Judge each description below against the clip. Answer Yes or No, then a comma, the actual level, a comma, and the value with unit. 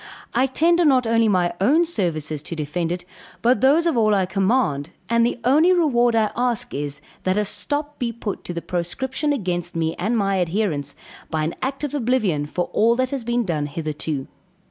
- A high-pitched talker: Yes, high, 215 Hz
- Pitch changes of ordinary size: No, wide, 7.3 semitones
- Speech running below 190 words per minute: No, average, 195 wpm